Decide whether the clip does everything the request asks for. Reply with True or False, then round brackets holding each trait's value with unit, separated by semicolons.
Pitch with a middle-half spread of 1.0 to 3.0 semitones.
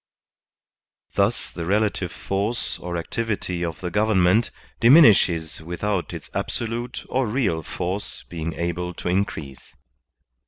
False (4.2 semitones)